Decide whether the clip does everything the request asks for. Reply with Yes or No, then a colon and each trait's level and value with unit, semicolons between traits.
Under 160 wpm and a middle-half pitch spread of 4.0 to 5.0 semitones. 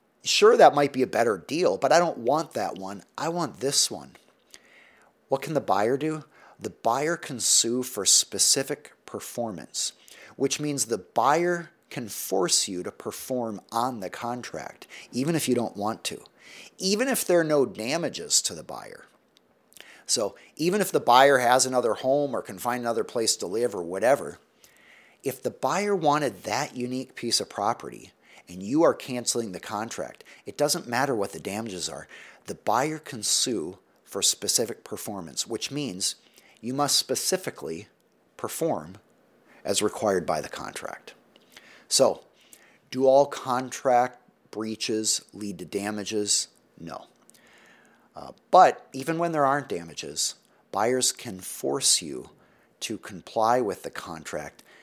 Yes: average, 150 wpm; average, 4.5 semitones